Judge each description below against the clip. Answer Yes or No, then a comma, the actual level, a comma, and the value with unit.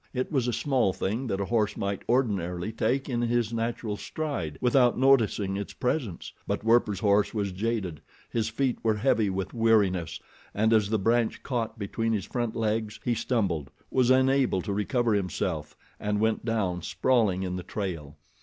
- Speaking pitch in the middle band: No, low, 110 Hz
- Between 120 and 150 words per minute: No, average, 175 wpm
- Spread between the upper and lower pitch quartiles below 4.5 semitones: Yes, average, 3.5 semitones